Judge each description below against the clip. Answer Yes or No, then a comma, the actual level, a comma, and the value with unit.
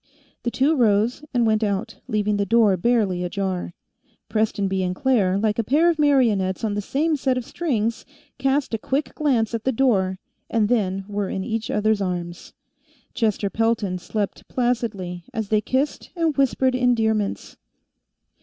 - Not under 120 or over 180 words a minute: Yes, average, 160 wpm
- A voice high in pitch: Yes, high, 220 Hz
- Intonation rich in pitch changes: No, average, 4.0 semitones